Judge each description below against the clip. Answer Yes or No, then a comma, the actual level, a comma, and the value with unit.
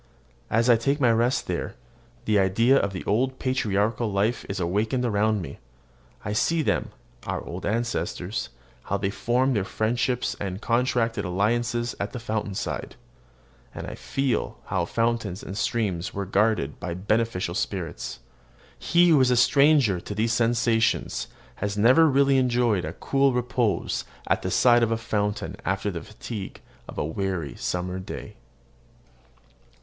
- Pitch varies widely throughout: No, average, 3.7 semitones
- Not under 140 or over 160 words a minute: Yes, average, 150 wpm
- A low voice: Yes, low, 110 Hz